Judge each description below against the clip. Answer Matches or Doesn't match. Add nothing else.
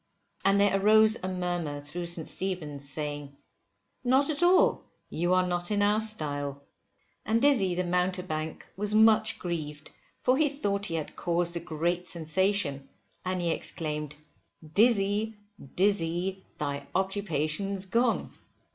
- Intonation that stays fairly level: Doesn't match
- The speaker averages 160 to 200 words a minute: Doesn't match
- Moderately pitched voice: Matches